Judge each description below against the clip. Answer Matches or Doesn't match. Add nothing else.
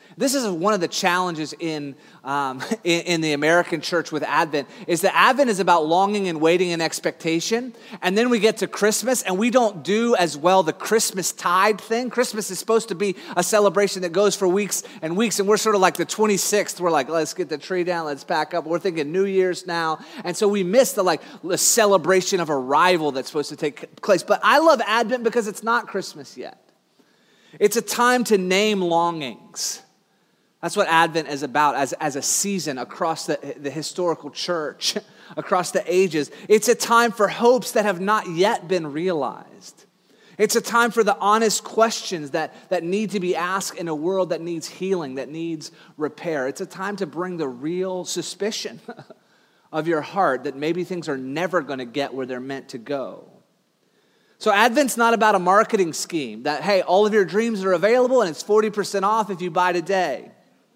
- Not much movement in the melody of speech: Doesn't match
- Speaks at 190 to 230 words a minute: Matches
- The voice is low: Doesn't match